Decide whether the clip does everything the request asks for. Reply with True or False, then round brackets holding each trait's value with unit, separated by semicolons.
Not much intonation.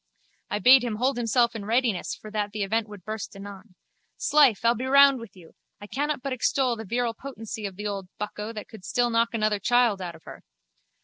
False (3.1 semitones)